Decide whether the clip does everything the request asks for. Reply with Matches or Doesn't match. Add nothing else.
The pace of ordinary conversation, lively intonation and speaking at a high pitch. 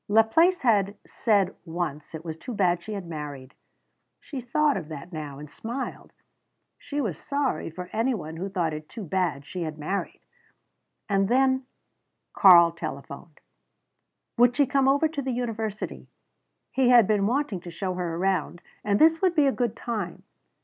Matches